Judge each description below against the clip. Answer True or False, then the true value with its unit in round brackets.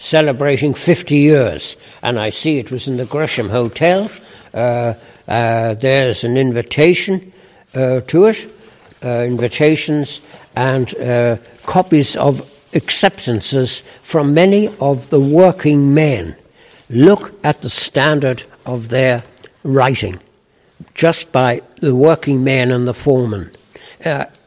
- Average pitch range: True (4.1 semitones)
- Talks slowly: True (120 wpm)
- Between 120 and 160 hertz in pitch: True (135 Hz)